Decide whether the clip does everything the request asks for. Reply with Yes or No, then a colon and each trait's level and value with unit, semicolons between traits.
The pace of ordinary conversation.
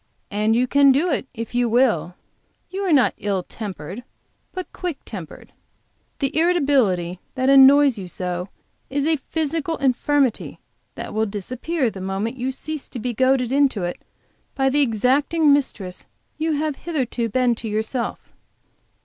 Yes: average, 150 wpm